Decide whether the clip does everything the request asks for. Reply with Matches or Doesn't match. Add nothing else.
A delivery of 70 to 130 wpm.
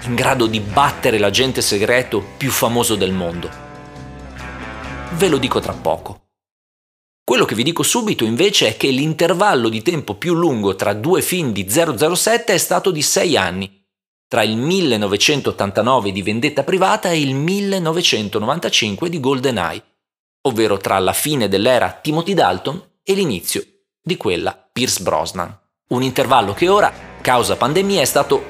Doesn't match